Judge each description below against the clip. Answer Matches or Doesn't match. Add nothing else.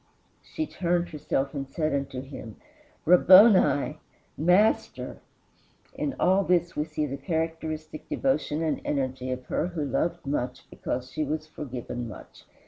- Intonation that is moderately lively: Matches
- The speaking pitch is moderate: Matches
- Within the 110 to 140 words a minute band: Matches